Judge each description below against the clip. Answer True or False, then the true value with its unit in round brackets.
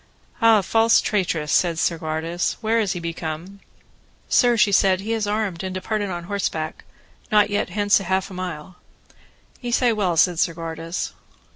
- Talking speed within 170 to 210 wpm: False (155 wpm)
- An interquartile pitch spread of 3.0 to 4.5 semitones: True (3.9 semitones)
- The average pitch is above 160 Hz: True (185 Hz)